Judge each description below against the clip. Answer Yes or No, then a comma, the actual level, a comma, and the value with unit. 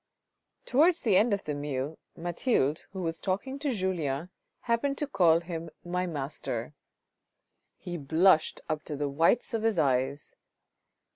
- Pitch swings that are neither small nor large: No, wide, 6.0 semitones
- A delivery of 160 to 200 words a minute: No, average, 150 wpm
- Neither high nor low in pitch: Yes, medium, 170 Hz